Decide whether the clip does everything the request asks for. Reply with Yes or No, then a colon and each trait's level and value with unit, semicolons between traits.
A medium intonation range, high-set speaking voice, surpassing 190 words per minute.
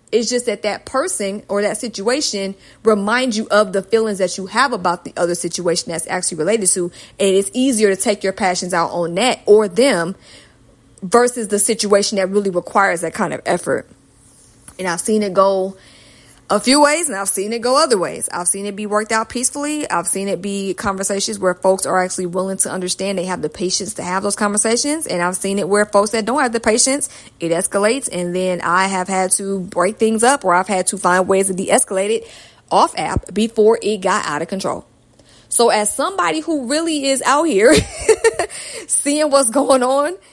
Yes: average, 4.1 semitones; high, 200 Hz; fast, 205 wpm